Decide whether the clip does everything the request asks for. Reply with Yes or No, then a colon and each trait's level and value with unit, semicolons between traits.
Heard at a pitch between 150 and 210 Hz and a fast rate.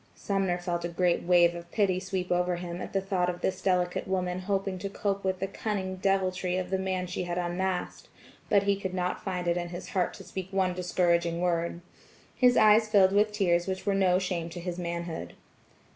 Yes: medium, 185 Hz; fast, 210 wpm